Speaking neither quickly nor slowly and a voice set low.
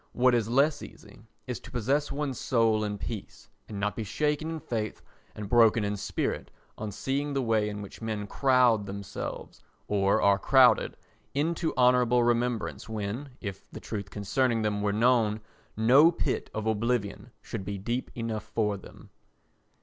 Yes: average, 165 wpm; low, 115 Hz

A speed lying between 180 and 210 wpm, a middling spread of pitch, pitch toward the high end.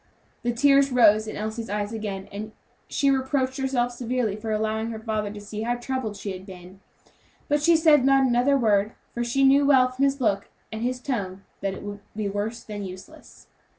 Yes: average, 195 wpm; average, 4.0 semitones; high, 225 Hz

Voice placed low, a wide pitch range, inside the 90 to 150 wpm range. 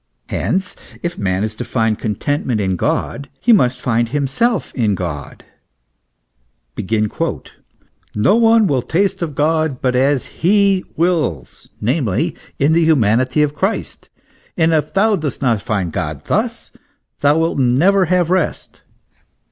No: medium, 145 Hz; wide, 7.7 semitones; average, 140 wpm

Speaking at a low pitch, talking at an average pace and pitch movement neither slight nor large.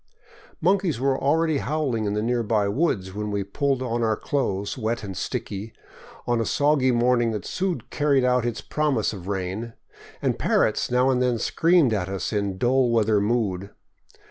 Yes: low, 120 Hz; average, 170 wpm; average, 4.5 semitones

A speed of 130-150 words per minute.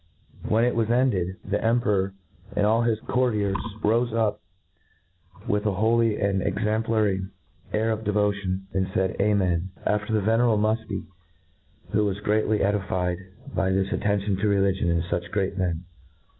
Yes: average, 145 wpm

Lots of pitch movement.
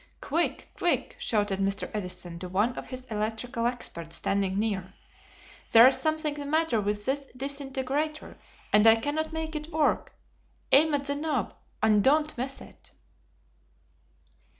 Yes: wide, 6.1 semitones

